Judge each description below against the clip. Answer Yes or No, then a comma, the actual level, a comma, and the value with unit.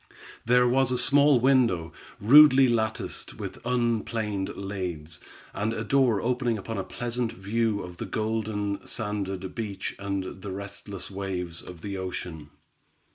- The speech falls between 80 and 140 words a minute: Yes, slow, 135 wpm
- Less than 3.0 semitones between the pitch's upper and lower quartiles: No, average, 3.9 semitones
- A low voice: Yes, low, 105 Hz